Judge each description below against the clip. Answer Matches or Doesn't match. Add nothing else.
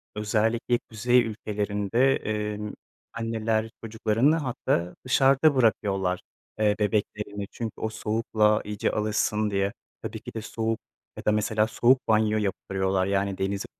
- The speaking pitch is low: Matches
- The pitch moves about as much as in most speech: Doesn't match